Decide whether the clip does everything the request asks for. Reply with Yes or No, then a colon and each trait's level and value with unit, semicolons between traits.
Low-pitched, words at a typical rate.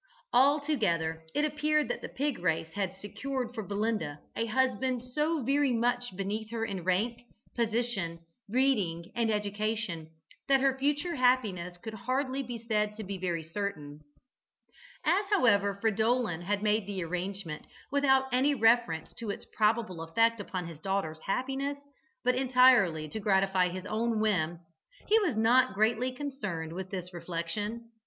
No: high, 220 Hz; average, 150 wpm